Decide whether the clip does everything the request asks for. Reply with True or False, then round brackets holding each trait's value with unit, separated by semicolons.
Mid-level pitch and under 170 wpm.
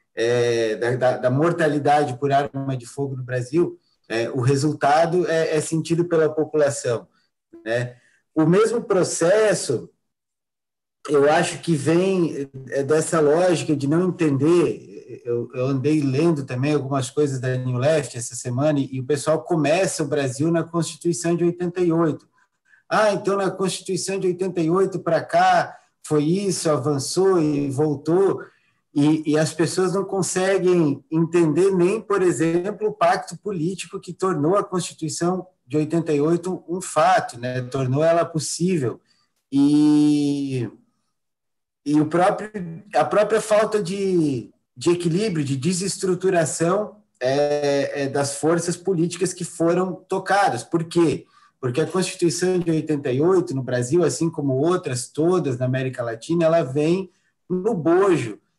True (165 Hz; 135 wpm)